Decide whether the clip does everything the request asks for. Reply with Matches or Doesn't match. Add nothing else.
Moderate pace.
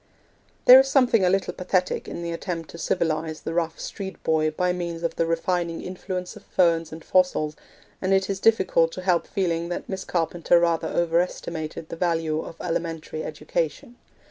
Matches